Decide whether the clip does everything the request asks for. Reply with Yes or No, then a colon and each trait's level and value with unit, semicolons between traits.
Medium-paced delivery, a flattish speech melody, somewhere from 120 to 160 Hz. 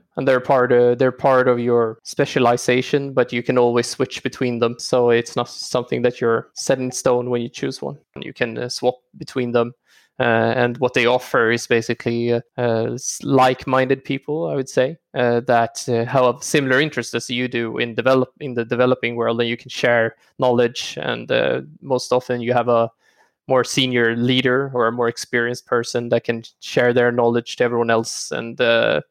Yes: average, 190 wpm; narrow, 1.6 semitones; low, 125 Hz